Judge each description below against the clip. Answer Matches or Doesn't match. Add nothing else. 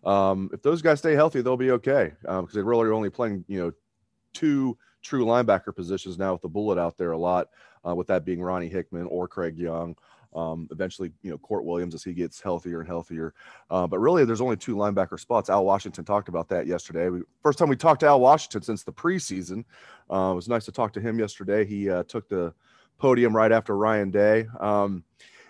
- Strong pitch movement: Doesn't match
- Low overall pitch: Matches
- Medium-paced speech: Doesn't match